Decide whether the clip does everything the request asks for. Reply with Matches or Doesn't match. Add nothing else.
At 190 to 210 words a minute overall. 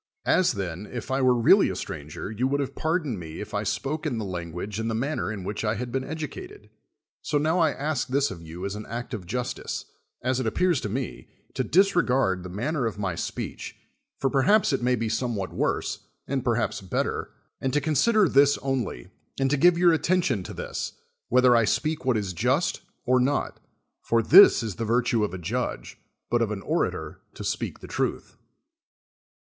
Matches